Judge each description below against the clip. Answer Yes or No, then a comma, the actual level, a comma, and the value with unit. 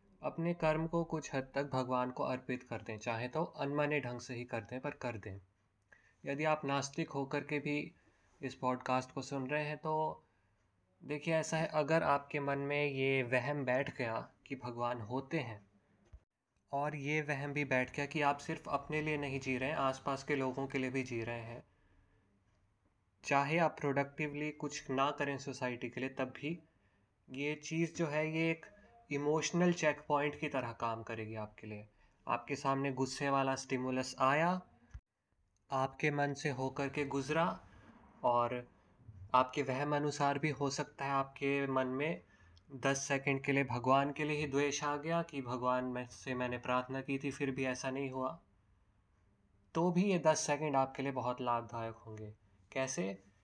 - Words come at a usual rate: Yes, average, 175 wpm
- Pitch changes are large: No, average, 3.4 semitones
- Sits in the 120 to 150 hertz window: Yes, low, 135 Hz